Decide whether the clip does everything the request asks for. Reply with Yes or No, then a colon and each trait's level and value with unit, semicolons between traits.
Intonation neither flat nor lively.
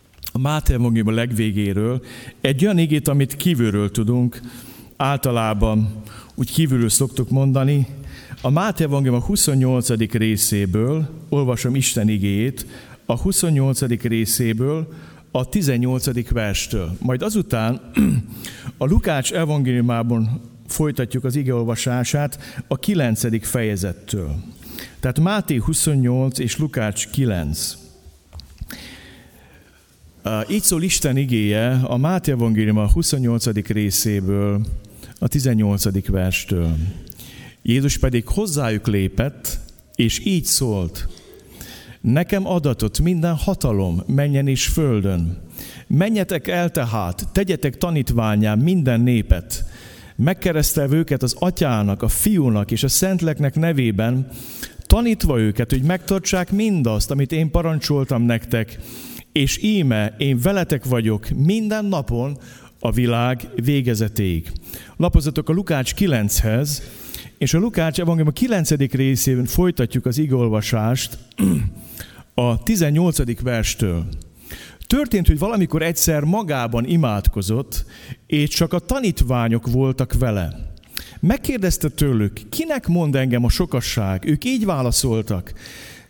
No: wide, 5.7 semitones